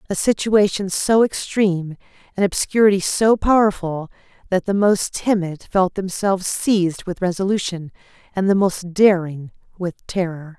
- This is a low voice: No, high, 190 Hz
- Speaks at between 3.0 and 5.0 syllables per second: Yes, 4.6 syllables/s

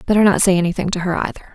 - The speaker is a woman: Yes, female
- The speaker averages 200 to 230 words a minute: No, fast, 275 wpm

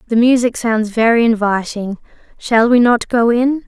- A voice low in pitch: No, high, 230 Hz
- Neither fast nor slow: Yes, average, 165 wpm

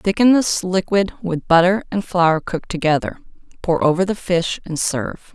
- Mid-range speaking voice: Yes, medium, 180 Hz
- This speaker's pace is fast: No, average, 170 wpm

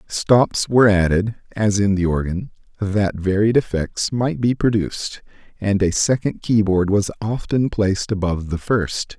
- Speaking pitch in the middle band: No, low, 105 Hz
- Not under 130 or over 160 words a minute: Yes, average, 150 wpm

